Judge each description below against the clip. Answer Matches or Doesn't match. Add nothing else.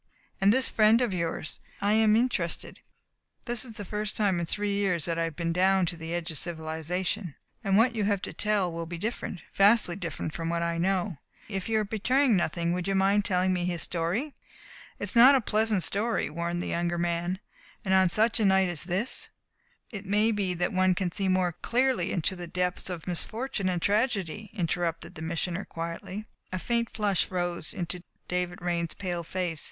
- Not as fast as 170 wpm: Doesn't match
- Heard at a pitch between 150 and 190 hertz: Matches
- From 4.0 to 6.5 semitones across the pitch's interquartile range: Doesn't match